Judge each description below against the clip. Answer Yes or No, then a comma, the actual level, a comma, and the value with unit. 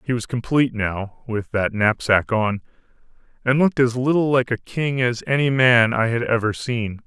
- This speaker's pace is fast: No, average, 185 wpm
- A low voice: Yes, low, 120 Hz